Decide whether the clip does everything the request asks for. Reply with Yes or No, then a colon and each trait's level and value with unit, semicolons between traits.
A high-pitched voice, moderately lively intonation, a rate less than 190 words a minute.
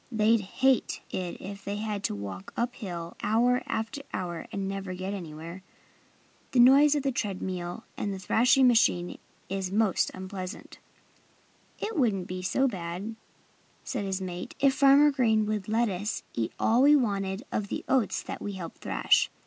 Yes: high, 200 Hz; average, 4.5 semitones; average, 170 wpm